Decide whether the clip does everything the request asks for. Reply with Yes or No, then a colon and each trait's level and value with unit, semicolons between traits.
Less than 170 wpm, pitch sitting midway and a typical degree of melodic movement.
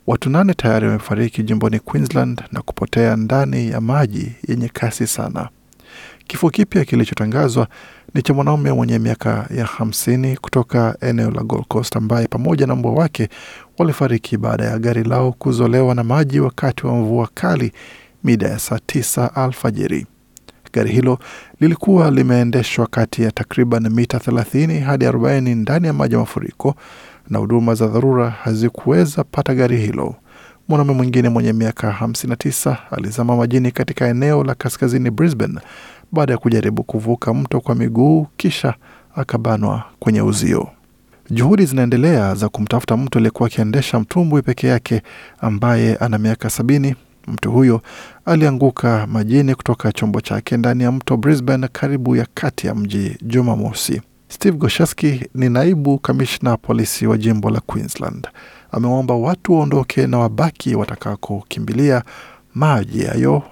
No: average, 135 wpm; low, 120 Hz; average, 3.1 semitones